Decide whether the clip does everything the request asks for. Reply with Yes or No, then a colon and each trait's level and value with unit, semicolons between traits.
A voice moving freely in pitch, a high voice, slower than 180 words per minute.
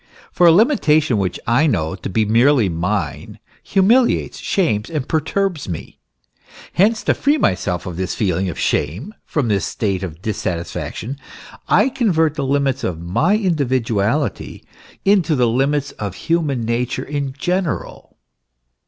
No: wide, 8.7 semitones; low, 135 Hz; average, 140 wpm